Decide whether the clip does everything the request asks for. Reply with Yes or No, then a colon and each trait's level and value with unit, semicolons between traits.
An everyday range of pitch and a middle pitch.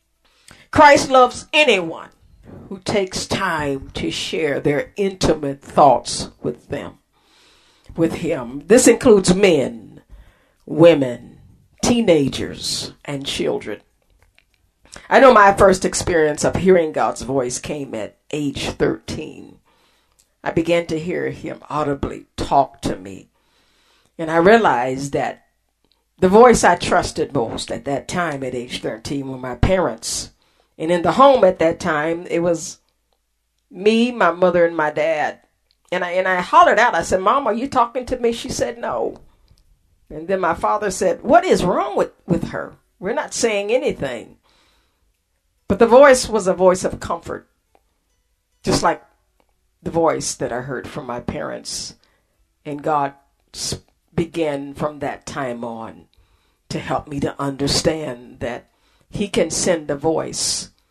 No: wide, 7.1 semitones; medium, 170 Hz